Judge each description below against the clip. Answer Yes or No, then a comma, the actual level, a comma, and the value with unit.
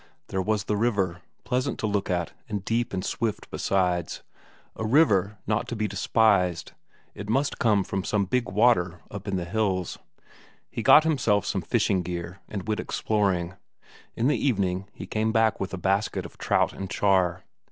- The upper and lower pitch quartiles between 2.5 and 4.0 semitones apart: Yes, average, 3.0 semitones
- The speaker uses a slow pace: No, average, 175 wpm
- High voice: No, low, 100 Hz